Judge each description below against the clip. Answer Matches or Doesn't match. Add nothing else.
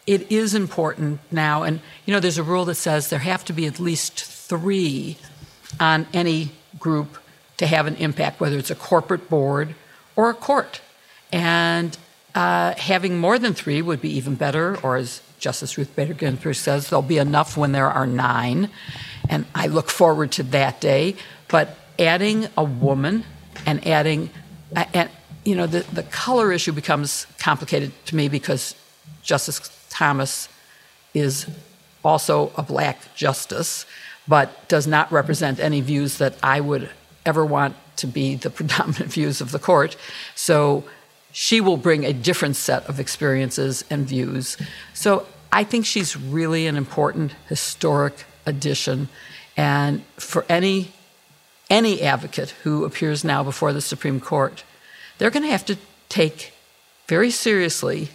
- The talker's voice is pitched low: Doesn't match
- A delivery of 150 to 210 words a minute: Matches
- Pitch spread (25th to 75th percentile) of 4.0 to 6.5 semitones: Doesn't match